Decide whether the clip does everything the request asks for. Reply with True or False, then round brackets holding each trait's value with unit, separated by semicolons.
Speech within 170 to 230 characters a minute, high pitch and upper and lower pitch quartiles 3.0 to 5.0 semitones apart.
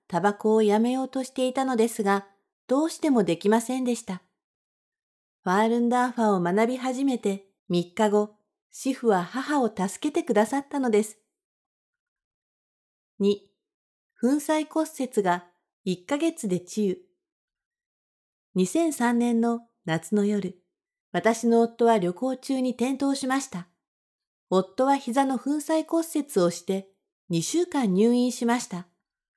False (225 characters per minute; 235 Hz; 5.5 semitones)